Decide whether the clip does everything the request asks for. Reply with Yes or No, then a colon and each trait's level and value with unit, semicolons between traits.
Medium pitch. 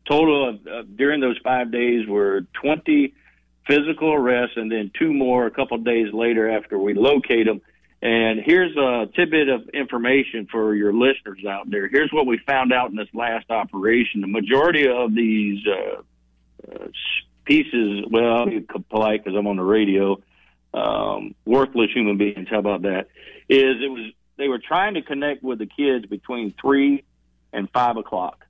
No: low, 115 Hz